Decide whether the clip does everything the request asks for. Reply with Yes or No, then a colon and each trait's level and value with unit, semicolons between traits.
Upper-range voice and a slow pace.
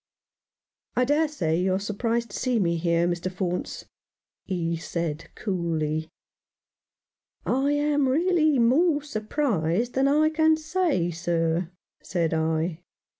Yes: high, 200 Hz; slow, 125 wpm